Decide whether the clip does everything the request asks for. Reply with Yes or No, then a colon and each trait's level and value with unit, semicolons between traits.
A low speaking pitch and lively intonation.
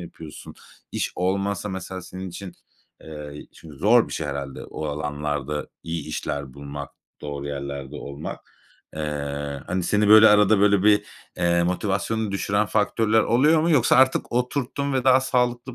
Yes: very low, 95 Hz; wide, 6.8 semitones